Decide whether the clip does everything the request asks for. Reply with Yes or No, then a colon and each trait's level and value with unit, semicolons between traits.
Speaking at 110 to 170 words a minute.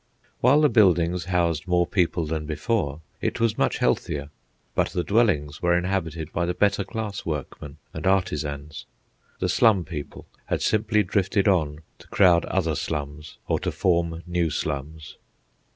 Yes: average, 150 wpm